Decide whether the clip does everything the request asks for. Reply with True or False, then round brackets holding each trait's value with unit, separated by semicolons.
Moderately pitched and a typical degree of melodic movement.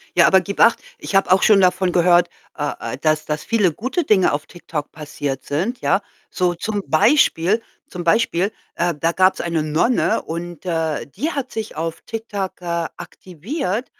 True (175 Hz; 4.2 semitones)